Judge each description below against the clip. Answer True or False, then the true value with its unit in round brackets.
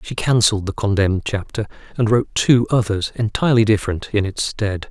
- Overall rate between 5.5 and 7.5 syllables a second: True (6.0 syllables/s)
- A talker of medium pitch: False (105 Hz)